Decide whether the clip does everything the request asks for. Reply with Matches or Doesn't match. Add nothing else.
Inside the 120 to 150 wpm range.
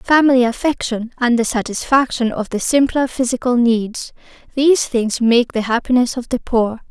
Matches